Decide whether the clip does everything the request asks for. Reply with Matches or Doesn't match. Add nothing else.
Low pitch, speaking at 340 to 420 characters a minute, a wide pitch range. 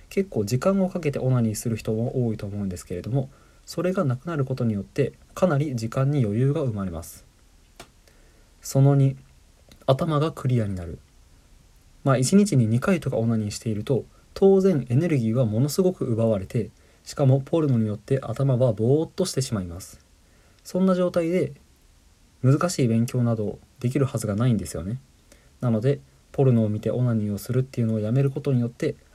Doesn't match